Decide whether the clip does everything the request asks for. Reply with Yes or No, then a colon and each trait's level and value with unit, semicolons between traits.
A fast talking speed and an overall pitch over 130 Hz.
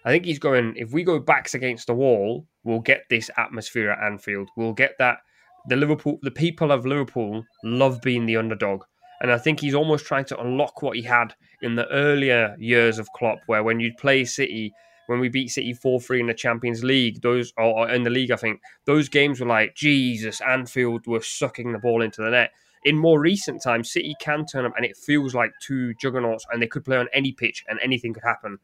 No: fast, 225 wpm; low, 125 Hz